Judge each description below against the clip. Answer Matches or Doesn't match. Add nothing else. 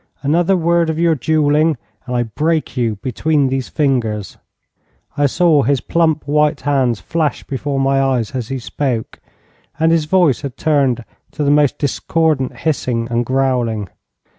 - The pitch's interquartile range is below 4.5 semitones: Matches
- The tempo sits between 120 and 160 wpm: Matches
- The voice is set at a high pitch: Doesn't match